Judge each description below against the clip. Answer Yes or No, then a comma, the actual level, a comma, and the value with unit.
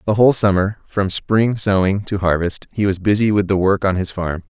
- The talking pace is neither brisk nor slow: No, fast, 225 wpm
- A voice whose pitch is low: Yes, low, 100 Hz